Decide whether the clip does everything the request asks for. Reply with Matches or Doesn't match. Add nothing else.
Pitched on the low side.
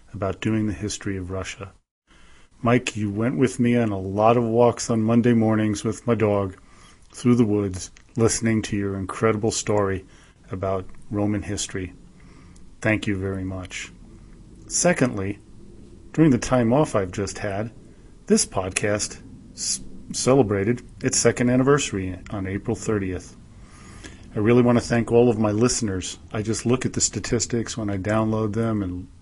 Matches